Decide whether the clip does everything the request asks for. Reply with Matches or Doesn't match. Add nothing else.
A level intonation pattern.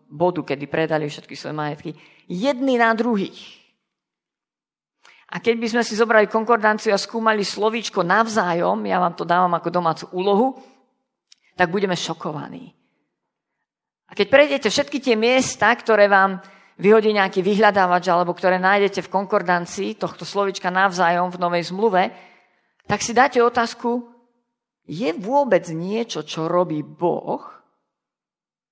Doesn't match